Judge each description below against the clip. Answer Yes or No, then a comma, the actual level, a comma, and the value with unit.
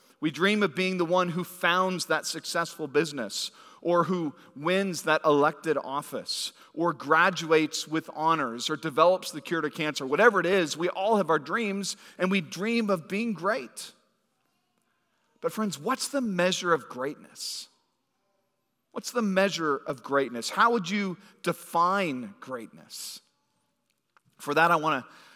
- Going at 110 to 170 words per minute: Yes, average, 150 wpm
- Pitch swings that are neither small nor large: Yes, average, 3.7 semitones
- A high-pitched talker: No, medium, 175 Hz